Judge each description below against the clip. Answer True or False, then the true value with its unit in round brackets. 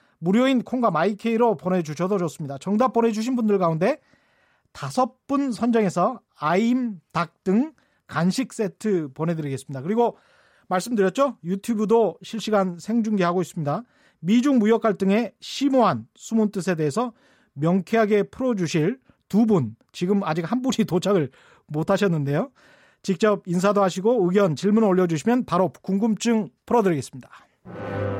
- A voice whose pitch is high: True (205 Hz)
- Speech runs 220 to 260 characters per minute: False (320 characters per minute)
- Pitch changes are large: False (5.0 semitones)